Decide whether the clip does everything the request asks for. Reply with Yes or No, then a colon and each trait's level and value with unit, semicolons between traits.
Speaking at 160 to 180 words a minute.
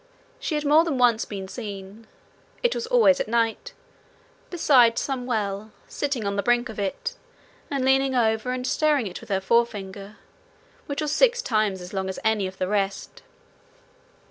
Yes: average, 170 wpm